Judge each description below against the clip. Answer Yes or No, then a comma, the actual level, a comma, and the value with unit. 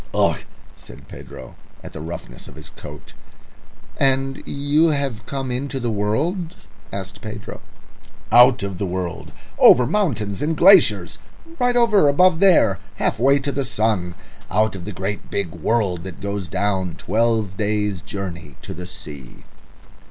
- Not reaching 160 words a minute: Yes, average, 150 wpm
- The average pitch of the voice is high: No, low, 110 Hz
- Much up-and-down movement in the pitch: Yes, wide, 6.5 semitones